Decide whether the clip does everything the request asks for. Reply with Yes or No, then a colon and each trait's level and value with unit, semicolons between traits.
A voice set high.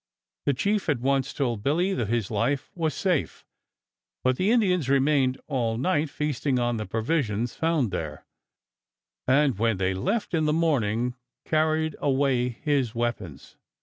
No: low, 135 Hz